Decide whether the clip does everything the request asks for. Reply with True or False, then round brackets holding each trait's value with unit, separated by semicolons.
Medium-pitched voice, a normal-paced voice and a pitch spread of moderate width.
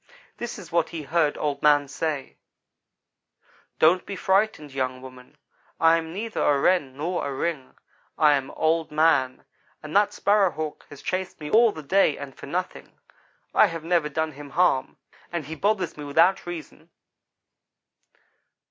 True (160 Hz; 160 wpm; 3.8 semitones)